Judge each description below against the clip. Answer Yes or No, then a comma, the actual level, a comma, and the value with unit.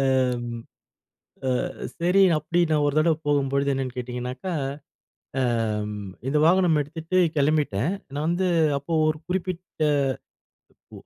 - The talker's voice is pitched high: No, medium, 145 Hz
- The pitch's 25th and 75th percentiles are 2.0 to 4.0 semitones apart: No, average, 4.8 semitones